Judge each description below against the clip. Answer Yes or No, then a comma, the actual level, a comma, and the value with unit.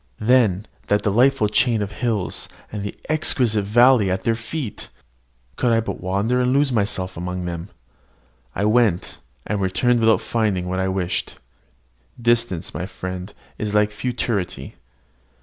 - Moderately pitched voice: No, low, 105 Hz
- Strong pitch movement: No, average, 4.1 semitones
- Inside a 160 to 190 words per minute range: No, average, 145 wpm